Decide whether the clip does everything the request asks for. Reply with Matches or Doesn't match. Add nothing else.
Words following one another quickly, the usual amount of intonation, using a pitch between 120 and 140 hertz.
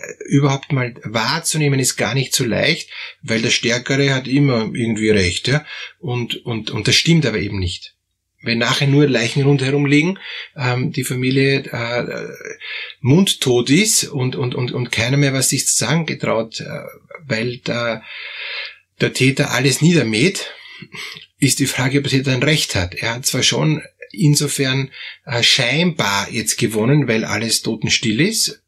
Doesn't match